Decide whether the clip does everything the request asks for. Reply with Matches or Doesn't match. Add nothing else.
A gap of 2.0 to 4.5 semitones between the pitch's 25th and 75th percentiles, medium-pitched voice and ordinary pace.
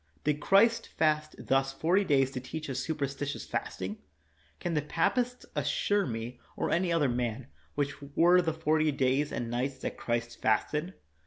Matches